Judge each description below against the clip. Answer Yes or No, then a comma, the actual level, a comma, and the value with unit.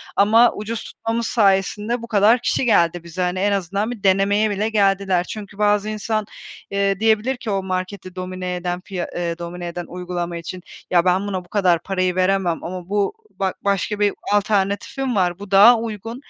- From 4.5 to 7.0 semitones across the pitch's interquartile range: No, narrow, 2.5 semitones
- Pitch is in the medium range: No, high, 195 Hz